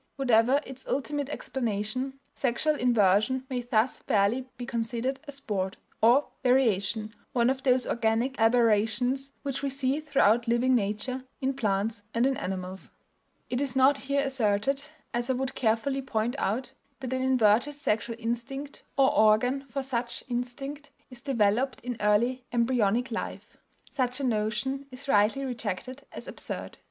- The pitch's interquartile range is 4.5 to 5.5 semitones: No, average, 3.2 semitones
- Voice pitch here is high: Yes, high, 245 Hz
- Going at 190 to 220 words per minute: No, average, 145 wpm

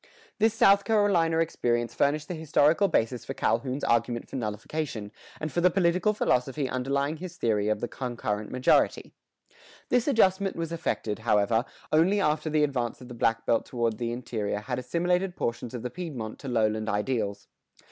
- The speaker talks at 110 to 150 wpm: No, average, 170 wpm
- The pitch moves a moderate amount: No, wide, 6.4 semitones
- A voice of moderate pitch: No, low, 130 Hz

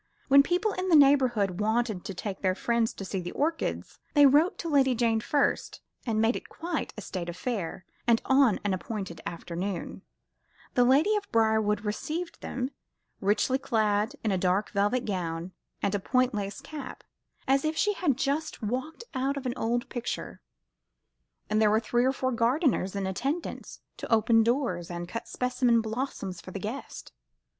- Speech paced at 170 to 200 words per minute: Yes, average, 175 wpm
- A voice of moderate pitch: No, high, 230 Hz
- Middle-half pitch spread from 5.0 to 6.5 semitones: Yes, average, 5.3 semitones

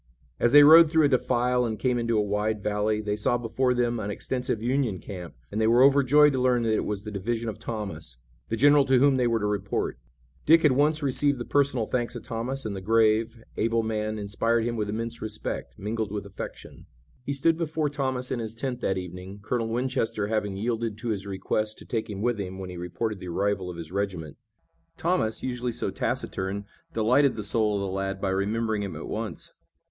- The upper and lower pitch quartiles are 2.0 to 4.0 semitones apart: Yes, average, 3.5 semitones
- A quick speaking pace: Yes, fast, 215 wpm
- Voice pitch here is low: Yes, low, 115 Hz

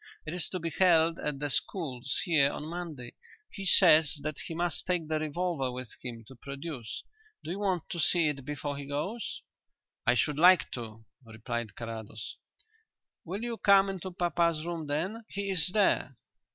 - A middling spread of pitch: Yes, average, 4.8 semitones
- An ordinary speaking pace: Yes, average, 175 wpm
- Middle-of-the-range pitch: Yes, medium, 155 Hz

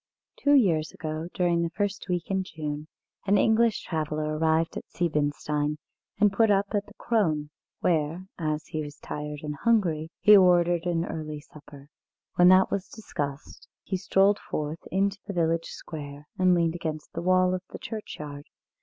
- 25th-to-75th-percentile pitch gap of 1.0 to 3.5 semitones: No, average, 4.0 semitones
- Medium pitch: Yes, medium, 170 Hz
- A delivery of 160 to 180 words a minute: Yes, average, 165 wpm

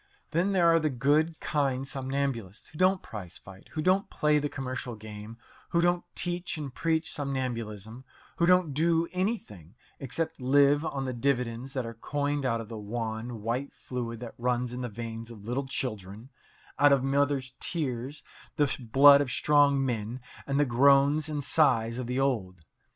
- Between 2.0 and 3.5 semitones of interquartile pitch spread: No, average, 4.0 semitones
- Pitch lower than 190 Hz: Yes, low, 135 Hz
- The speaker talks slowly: No, average, 175 wpm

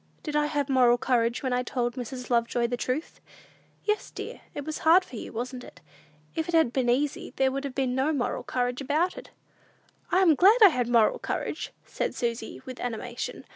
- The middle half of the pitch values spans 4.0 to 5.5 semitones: No, average, 3.5 semitones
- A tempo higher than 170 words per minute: Yes, fast, 205 wpm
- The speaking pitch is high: Yes, very high, 255 Hz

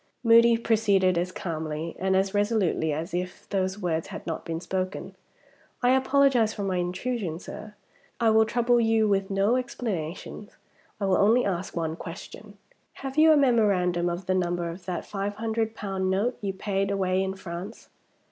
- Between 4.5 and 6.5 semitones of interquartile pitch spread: No, average, 3.8 semitones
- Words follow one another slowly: No, average, 170 wpm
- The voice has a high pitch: Yes, high, 195 Hz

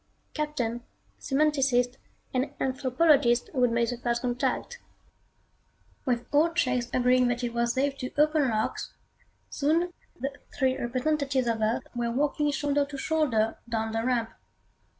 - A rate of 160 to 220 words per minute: No, slow, 135 wpm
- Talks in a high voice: Yes, very high, 255 Hz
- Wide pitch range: No, average, 3.3 semitones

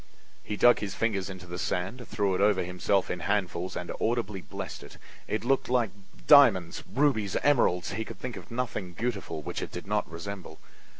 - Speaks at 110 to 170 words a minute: No, average, 185 wpm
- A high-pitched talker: No, low, 100 Hz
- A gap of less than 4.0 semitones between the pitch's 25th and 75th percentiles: No, average, 4.3 semitones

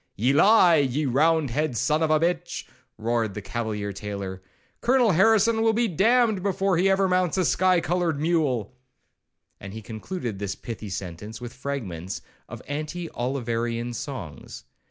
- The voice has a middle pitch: Yes, medium, 145 Hz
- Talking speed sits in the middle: Yes, average, 160 wpm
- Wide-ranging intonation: Yes, wide, 8.5 semitones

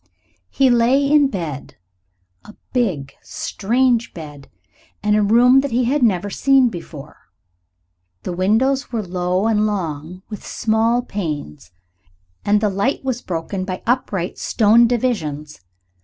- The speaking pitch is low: No, high, 210 Hz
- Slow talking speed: Yes, slow, 130 wpm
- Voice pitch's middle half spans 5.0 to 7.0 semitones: Yes, wide, 5.5 semitones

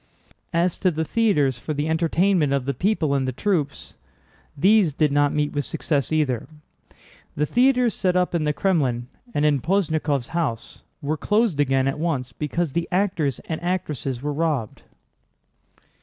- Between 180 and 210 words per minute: No, average, 160 wpm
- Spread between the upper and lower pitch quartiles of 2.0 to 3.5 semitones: No, average, 4.2 semitones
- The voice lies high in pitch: No, medium, 155 Hz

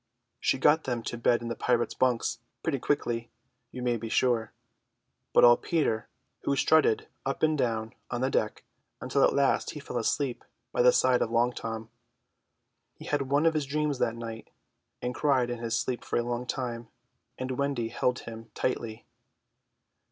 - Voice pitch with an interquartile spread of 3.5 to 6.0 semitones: No, average, 2.9 semitones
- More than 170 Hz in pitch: No, low, 125 Hz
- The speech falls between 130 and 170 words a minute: No, average, 180 wpm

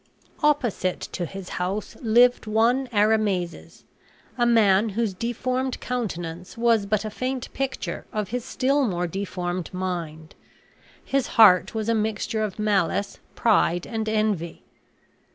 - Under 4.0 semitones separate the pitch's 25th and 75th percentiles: No, average, 4.3 semitones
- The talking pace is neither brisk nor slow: No, slow, 130 wpm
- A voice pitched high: Yes, high, 215 Hz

